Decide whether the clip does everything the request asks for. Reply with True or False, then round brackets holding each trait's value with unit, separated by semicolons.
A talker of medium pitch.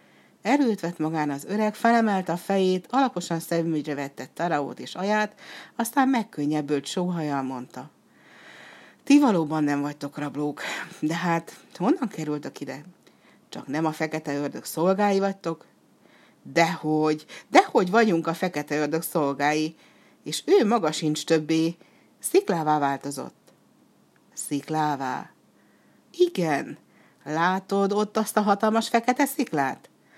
True (165 Hz)